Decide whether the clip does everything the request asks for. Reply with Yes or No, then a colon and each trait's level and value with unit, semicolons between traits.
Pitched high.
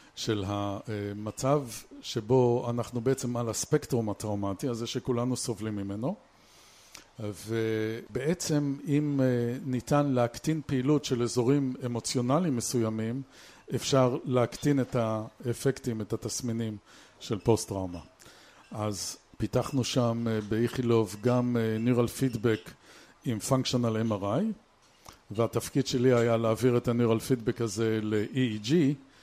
No: low, 120 Hz